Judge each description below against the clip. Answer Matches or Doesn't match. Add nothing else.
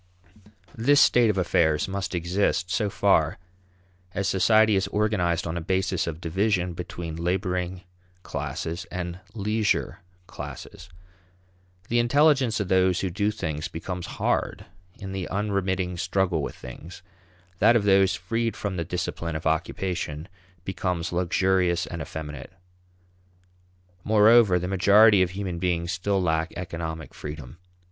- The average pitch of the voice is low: Matches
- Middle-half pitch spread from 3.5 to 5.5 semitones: Doesn't match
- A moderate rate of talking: Doesn't match